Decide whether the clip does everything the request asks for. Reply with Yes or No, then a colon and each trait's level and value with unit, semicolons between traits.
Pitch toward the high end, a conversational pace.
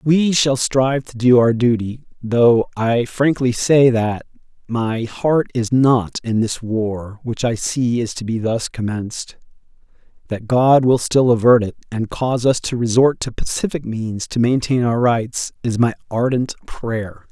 No: low, 120 Hz; average, 170 wpm